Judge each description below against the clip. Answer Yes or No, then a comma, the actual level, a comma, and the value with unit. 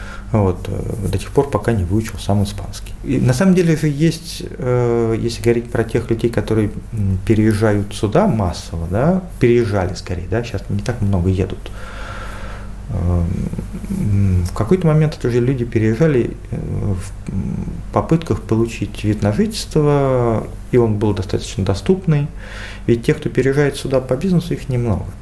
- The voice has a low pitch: Yes, low, 110 Hz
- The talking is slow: No, average, 145 wpm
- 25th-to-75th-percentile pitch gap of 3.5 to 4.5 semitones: Yes, average, 3.9 semitones